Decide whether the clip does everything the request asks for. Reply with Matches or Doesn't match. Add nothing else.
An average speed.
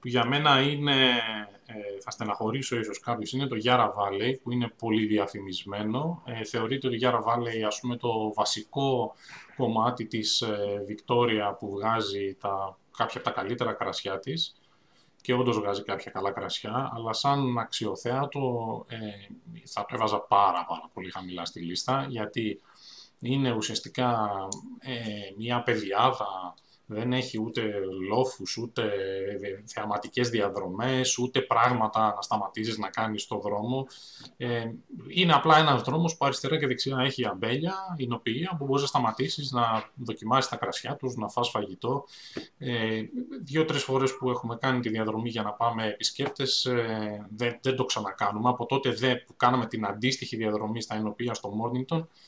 Matches